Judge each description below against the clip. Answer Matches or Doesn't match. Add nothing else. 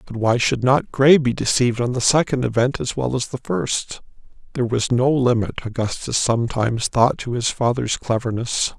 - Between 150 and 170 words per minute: Doesn't match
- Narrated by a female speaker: Doesn't match